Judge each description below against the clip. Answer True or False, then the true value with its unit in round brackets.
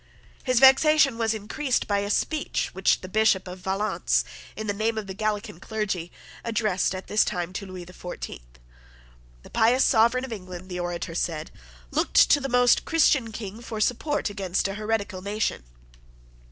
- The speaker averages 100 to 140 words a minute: False (170 wpm)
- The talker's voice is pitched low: False (210 Hz)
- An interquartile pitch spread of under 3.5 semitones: False (3.8 semitones)